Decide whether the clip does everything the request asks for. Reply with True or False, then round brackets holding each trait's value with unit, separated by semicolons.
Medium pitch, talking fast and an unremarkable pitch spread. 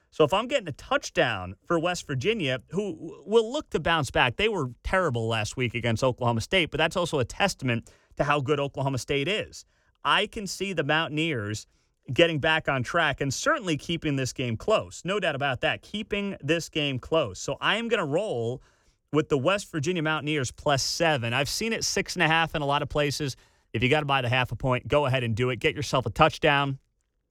True (145 Hz; 220 wpm; 4.6 semitones)